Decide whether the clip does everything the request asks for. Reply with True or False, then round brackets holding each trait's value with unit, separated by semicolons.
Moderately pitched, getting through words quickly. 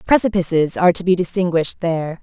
False (175 Hz; 160 wpm)